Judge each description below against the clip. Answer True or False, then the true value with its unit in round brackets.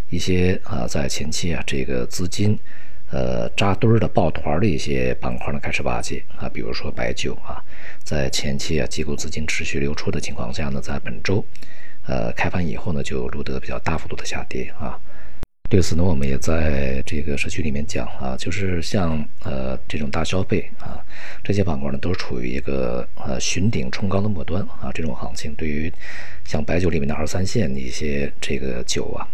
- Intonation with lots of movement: False (4.9 semitones)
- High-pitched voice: False (75 Hz)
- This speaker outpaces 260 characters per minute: True (290 characters per minute)